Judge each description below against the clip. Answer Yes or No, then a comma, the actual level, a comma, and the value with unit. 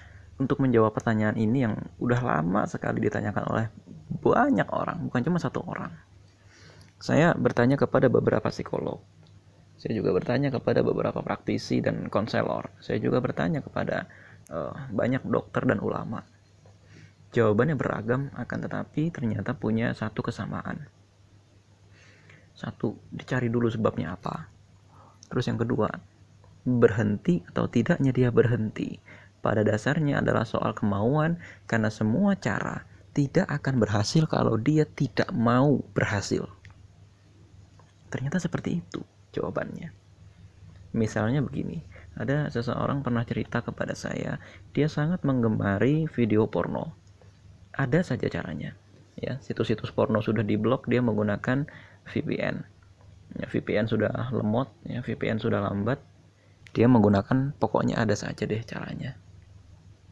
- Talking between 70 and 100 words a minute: No, average, 120 wpm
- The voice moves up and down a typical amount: Yes, average, 4.2 semitones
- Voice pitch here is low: Yes, low, 110 Hz